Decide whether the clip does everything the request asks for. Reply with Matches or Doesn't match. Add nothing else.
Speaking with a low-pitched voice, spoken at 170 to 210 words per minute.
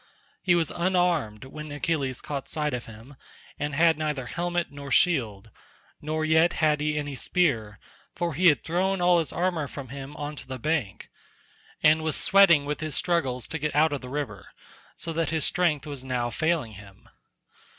Doesn't match